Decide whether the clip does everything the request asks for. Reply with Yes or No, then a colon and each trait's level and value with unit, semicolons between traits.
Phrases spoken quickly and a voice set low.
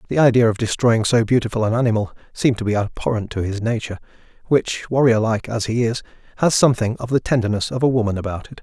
Yes: fast, 215 wpm; low, 115 Hz